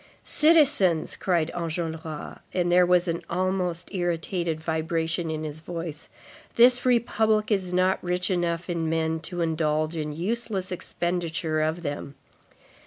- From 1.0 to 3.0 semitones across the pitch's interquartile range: Yes, narrow, 2.4 semitones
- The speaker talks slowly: Yes, slow, 130 wpm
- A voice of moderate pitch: Yes, medium, 170 Hz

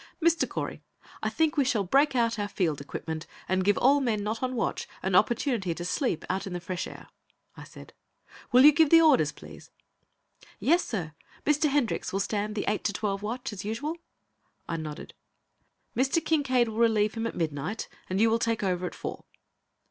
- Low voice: No, high, 225 Hz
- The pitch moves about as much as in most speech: No, wide, 5.9 semitones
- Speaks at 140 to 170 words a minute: No, average, 195 wpm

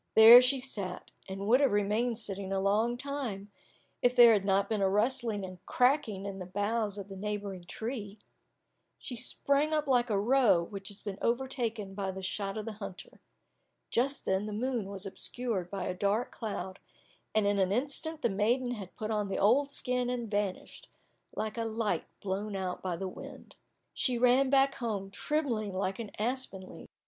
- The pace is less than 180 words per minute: No, average, 185 wpm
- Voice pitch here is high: Yes, high, 215 Hz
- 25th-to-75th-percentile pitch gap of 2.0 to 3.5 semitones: No, average, 3.9 semitones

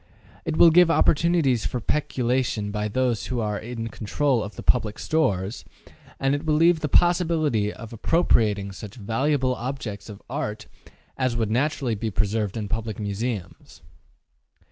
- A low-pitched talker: Yes, low, 120 Hz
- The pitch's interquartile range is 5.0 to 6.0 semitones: Yes, wide, 5.5 semitones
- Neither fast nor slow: Yes, average, 150 wpm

